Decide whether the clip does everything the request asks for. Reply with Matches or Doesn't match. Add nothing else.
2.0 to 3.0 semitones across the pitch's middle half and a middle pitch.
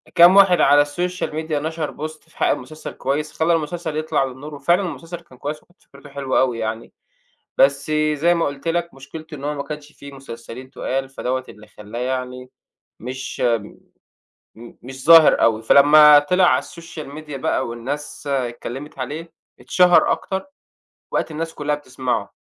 Doesn't match